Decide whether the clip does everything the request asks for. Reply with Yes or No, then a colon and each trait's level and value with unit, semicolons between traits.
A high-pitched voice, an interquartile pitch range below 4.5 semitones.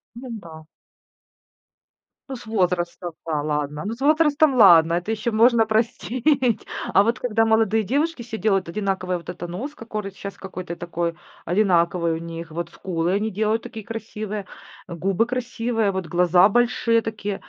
No: high, 205 Hz; average, 4.8 semitones